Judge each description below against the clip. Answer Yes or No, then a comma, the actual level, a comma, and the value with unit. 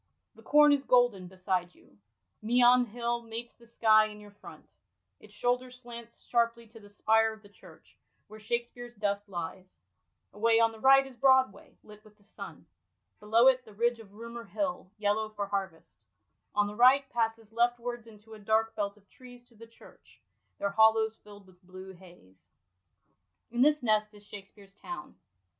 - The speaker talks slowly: No, average, 175 wpm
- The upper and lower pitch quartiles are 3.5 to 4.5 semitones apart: No, average, 2.8 semitones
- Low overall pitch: No, high, 225 Hz